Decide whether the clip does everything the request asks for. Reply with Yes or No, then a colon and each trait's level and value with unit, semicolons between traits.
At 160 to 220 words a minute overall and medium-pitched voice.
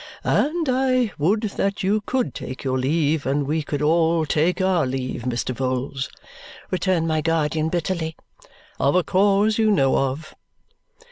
No: average, 150 wpm; medium, 160 Hz